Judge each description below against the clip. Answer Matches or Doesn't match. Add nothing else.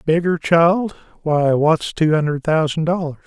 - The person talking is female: Doesn't match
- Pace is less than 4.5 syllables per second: Matches